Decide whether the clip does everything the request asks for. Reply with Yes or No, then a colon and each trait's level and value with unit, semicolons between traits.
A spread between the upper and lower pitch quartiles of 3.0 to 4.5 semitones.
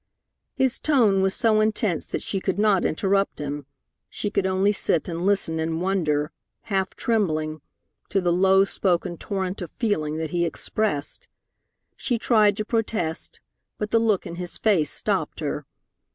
Yes: average, 4.0 semitones